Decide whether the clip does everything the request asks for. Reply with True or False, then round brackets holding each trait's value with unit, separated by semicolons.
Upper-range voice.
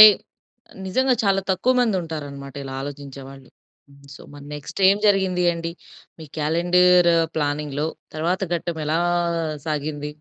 False (160 Hz)